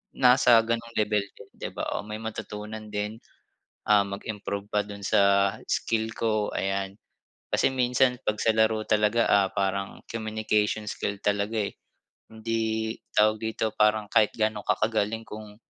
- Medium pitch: No, low, 110 Hz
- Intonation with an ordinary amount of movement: No, narrow, 1.3 semitones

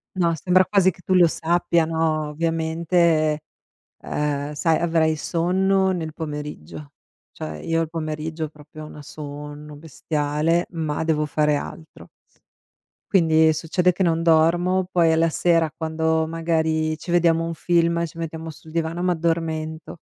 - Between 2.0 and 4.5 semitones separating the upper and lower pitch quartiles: No, narrow, 1.5 semitones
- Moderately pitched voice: Yes, medium, 160 Hz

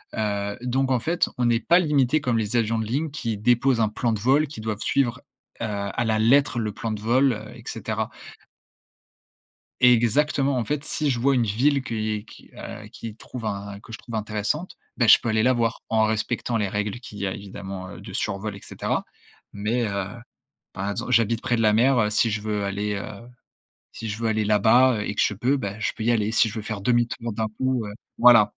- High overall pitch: No, low, 115 Hz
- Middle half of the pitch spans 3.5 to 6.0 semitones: No, average, 2.8 semitones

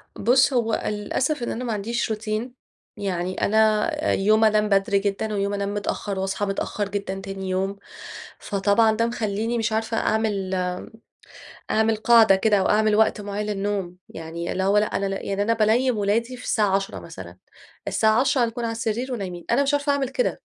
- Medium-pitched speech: No, high, 210 Hz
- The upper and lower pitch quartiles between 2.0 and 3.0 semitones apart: Yes, narrow, 2.5 semitones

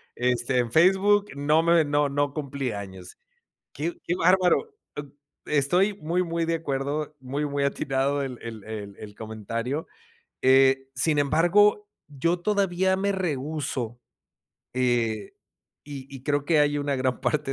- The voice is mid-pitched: Yes, medium, 145 Hz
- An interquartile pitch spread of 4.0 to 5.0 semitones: Yes, average, 4.3 semitones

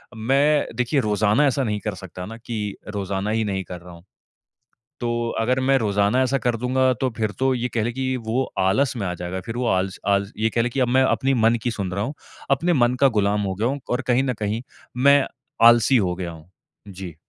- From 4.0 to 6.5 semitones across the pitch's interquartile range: Yes, average, 4.5 semitones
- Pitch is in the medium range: No, low, 115 Hz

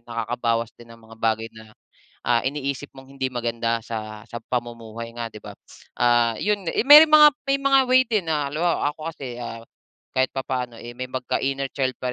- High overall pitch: No, low, 125 Hz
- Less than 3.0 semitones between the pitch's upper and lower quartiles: No, average, 3.9 semitones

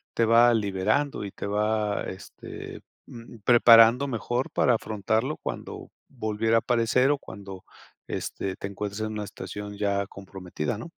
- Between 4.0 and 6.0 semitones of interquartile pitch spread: No, average, 2.7 semitones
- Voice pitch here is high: No, low, 110 Hz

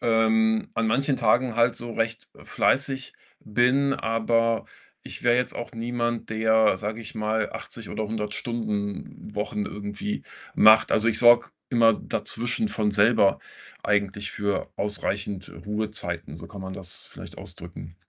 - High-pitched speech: No, low, 110 Hz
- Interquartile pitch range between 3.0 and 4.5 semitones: No, narrow, 2.4 semitones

